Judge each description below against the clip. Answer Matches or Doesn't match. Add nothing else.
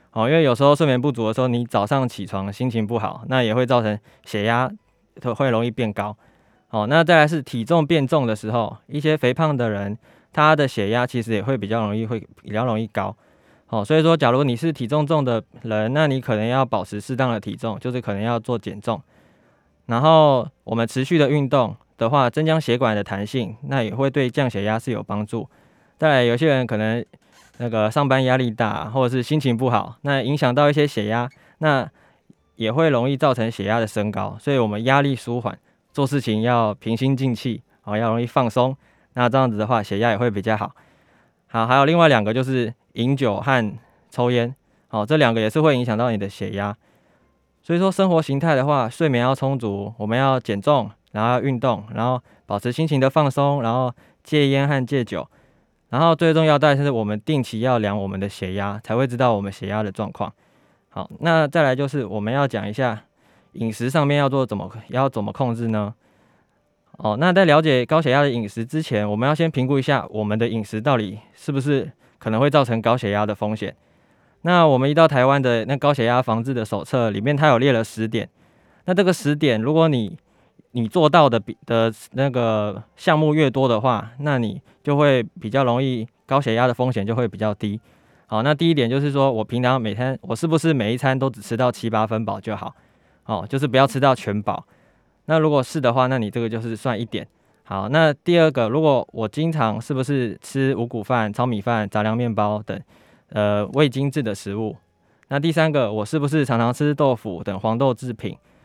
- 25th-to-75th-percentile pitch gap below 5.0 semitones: Matches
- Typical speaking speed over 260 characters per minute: Matches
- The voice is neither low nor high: Doesn't match